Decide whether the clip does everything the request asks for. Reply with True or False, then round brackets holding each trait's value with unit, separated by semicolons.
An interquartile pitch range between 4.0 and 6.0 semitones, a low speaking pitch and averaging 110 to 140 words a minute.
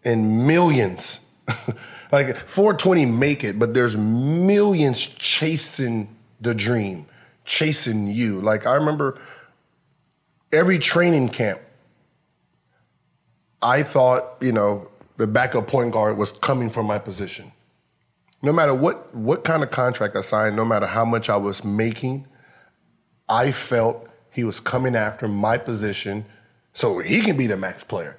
True (4.5 semitones; 120 Hz; 135 wpm)